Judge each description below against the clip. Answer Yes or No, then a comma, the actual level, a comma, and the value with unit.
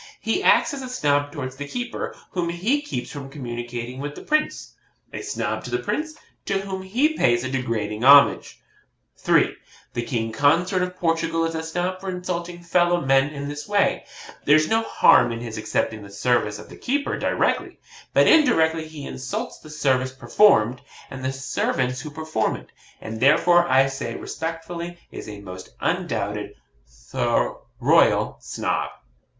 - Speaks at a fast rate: No, average, 165 wpm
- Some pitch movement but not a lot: No, wide, 5.7 semitones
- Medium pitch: Yes, medium, 150 Hz